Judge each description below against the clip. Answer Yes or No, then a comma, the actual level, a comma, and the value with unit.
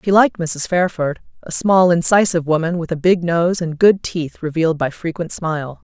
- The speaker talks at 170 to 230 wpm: Yes, average, 195 wpm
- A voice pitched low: No, medium, 170 Hz